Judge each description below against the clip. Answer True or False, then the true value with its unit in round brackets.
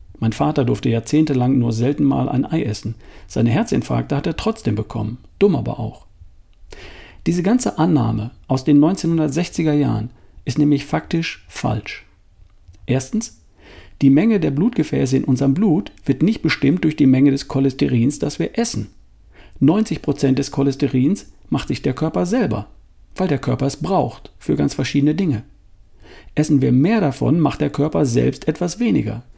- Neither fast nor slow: True (155 wpm)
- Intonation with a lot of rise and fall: True (5.7 semitones)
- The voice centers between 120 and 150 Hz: True (135 Hz)